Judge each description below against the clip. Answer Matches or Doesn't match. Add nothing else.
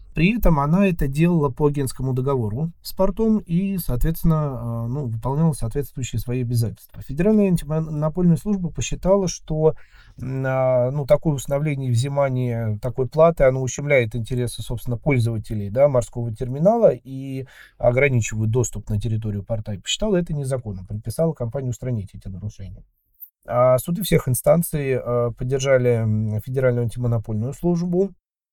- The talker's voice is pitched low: Matches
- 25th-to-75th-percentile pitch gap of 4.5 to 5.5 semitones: Matches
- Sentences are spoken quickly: Doesn't match